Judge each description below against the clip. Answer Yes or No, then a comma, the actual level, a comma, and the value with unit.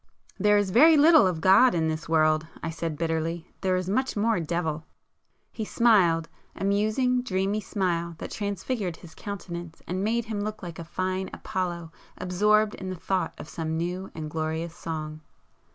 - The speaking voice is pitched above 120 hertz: Yes, medium, 185 Hz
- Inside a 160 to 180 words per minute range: Yes, average, 165 wpm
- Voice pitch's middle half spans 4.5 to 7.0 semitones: No, average, 4.1 semitones